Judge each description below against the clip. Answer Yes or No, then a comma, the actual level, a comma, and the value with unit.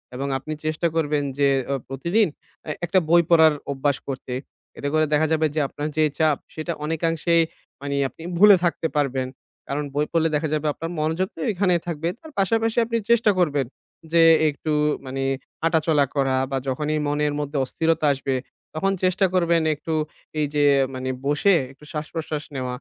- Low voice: No, medium, 155 Hz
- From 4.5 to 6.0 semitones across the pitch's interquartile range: No, average, 2.8 semitones